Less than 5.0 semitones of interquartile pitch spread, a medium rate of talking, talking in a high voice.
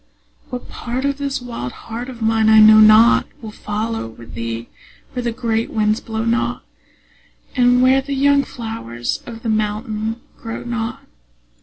Yes: narrow, 2.4 semitones; average, 160 wpm; high, 225 Hz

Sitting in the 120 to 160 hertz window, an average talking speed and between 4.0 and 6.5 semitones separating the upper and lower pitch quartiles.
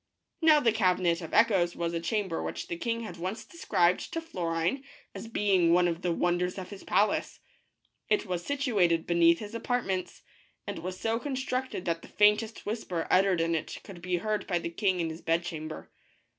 No: medium, 185 Hz; average, 185 wpm; average, 4.4 semitones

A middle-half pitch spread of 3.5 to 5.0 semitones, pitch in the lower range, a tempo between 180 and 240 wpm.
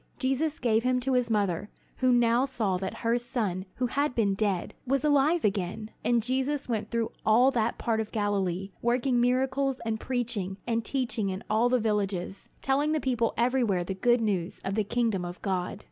No: average, 3.9 semitones; high, 230 Hz; average, 190 wpm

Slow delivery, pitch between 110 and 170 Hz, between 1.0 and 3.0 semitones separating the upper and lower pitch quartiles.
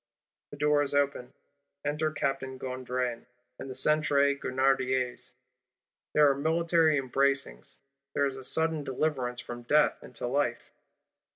Yes: slow, 125 wpm; low, 135 Hz; narrow, 2.5 semitones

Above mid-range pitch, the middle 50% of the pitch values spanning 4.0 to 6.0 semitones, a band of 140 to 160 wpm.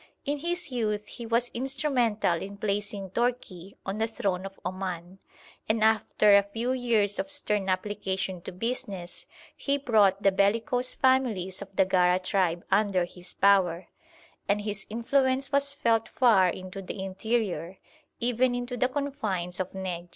Yes: high, 205 Hz; average, 4.5 semitones; average, 150 wpm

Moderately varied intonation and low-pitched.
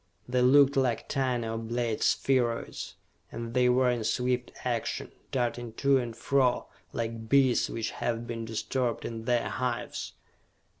No: narrow, 1.8 semitones; low, 120 Hz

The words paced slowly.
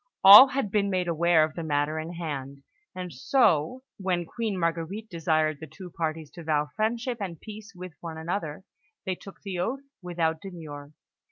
No: average, 175 wpm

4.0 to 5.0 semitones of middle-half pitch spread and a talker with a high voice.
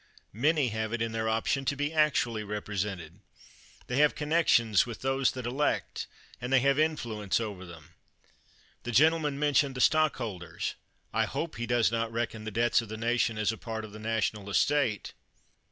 No: average, 4.3 semitones; low, 115 Hz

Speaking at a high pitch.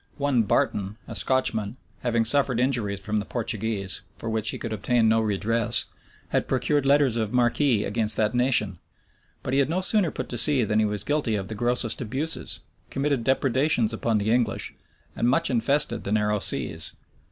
No: low, 115 Hz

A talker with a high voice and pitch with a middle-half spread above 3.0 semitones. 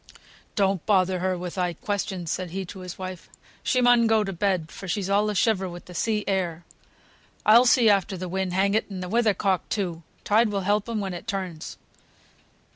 No: high, 195 Hz; narrow, 2.4 semitones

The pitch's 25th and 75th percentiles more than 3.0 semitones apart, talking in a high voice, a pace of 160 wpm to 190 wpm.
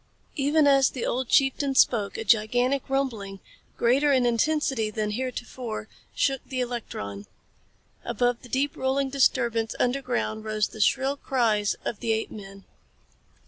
No: average, 3.7 semitones; high, 245 Hz; average, 140 wpm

